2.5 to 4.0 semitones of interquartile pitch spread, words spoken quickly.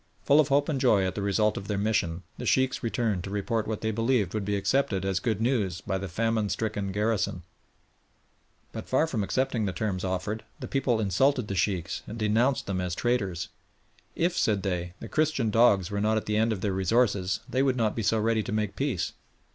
Yes: average, 3.5 semitones; fast, 215 wpm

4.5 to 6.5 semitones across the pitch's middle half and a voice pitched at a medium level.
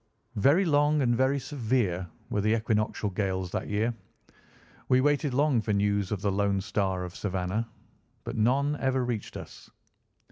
No: average, 4.9 semitones; low, 110 Hz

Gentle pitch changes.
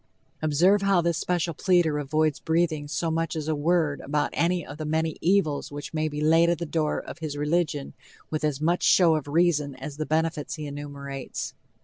Yes: narrow, 2.3 semitones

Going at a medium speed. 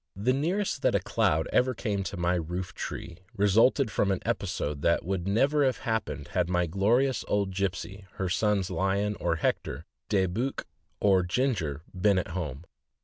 Yes: average, 170 wpm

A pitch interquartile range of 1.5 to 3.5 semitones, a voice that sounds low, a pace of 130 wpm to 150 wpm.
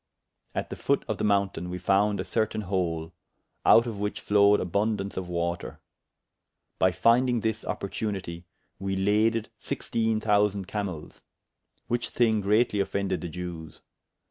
Yes: average, 3.1 semitones; low, 100 Hz; average, 140 wpm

